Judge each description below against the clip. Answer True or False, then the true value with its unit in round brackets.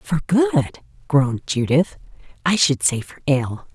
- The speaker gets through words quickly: False (145 wpm)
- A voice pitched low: False (150 Hz)